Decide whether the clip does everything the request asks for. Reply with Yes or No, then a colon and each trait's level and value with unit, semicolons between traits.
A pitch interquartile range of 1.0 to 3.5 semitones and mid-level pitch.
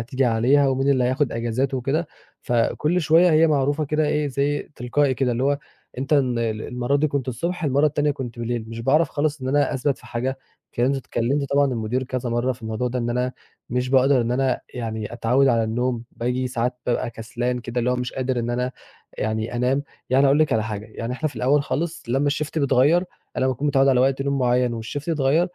No: average, 2.9 semitones; low, 130 Hz